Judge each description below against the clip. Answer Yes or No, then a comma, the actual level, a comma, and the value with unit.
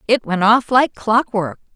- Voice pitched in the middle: No, high, 220 Hz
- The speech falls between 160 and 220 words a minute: Yes, fast, 205 wpm